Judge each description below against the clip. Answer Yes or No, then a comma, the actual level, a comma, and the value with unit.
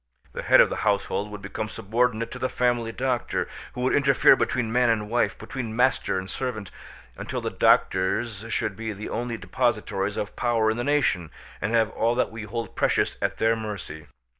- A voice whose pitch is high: No, low, 115 Hz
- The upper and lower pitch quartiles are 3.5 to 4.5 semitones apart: No, average, 2.7 semitones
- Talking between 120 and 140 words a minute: No, average, 190 wpm